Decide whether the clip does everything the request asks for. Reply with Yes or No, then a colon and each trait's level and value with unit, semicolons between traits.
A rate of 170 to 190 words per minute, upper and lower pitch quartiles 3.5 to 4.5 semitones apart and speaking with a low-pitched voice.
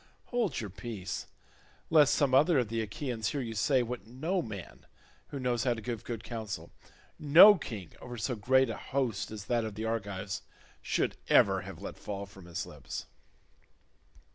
Yes: average, 175 wpm; average, 4.1 semitones; low, 115 Hz